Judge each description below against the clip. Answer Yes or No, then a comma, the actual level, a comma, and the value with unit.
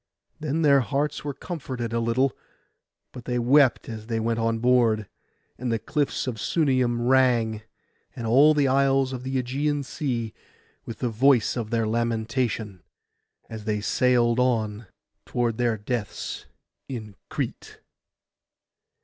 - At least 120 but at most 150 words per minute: Yes, average, 140 wpm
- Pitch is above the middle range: No, low, 120 Hz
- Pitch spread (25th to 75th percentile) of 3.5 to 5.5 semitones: No, average, 2.8 semitones